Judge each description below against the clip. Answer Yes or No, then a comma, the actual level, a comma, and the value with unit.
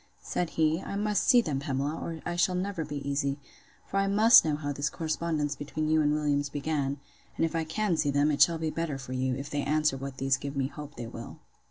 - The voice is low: No, medium, 150 Hz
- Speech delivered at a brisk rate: Yes, fast, 240 wpm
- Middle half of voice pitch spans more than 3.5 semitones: No, average, 2.7 semitones